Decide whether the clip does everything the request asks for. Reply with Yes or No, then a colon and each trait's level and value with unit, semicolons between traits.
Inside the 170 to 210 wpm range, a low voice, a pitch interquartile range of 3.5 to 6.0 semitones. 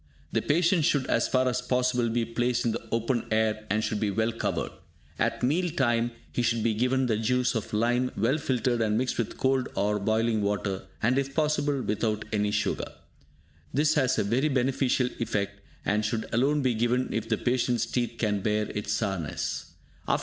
No: average, 185 wpm; low, 115 Hz; average, 3.0 semitones